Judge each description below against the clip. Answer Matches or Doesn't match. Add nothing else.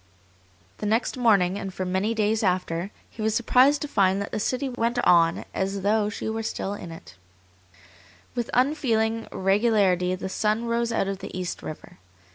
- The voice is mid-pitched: Doesn't match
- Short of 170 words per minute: Doesn't match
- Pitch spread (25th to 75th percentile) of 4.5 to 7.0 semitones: Doesn't match